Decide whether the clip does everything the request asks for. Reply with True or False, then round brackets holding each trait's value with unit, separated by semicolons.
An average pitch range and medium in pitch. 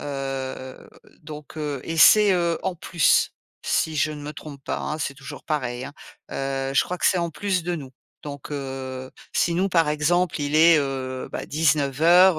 True (3.6 semitones; 150 Hz)